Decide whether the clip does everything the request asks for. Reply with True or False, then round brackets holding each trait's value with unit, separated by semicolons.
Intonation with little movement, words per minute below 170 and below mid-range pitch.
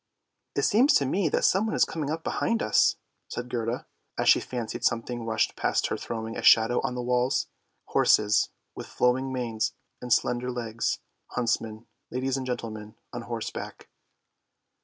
True (2.3 semitones; 160 wpm; 120 Hz)